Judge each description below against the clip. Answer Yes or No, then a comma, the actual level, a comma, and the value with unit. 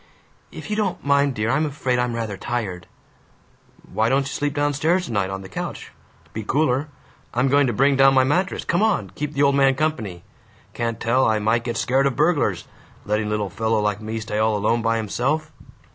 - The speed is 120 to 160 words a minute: No, fast, 205 wpm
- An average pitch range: Yes, average, 4.7 semitones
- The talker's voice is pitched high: No, low, 125 Hz